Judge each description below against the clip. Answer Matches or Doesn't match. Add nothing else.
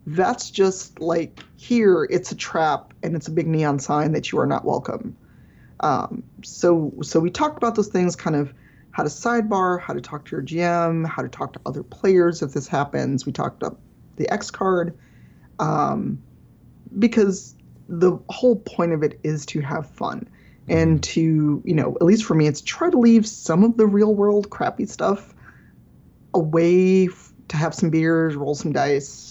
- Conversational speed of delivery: Matches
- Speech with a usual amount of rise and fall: Matches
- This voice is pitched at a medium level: Matches